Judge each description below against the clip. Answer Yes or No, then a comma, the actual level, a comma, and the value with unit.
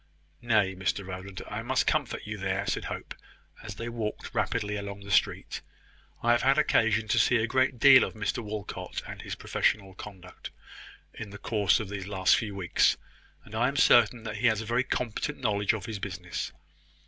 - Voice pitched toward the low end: Yes, low, 105 Hz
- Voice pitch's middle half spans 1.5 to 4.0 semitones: Yes, average, 2.7 semitones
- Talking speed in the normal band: Yes, average, 195 wpm